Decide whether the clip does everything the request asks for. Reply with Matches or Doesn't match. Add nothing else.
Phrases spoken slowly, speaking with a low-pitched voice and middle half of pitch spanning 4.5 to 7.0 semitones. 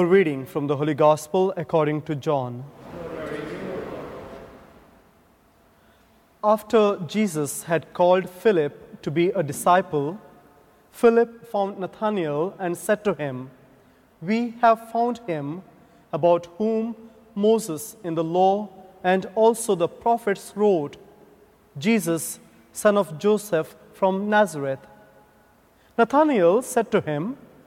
Doesn't match